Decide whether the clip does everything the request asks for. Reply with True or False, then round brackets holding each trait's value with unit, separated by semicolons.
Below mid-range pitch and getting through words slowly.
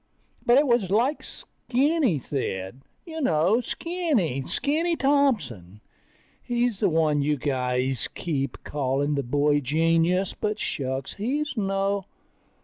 False (180 Hz; 120 wpm)